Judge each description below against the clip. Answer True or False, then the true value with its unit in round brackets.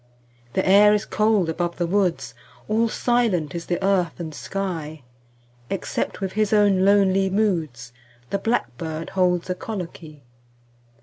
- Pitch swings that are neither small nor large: True (3.5 semitones)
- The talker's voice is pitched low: False (190 Hz)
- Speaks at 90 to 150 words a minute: True (140 wpm)